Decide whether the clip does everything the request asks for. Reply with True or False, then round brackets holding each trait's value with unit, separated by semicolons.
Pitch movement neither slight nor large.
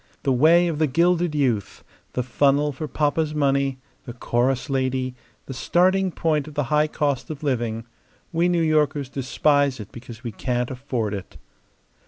True (3.4 semitones)